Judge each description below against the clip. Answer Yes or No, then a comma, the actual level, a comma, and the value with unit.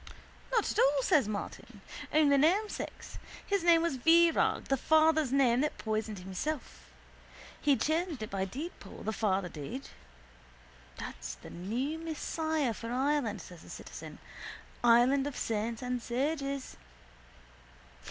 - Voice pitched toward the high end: Yes, very high, 270 Hz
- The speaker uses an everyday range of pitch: No, wide, 6.2 semitones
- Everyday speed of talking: No, slow, 130 wpm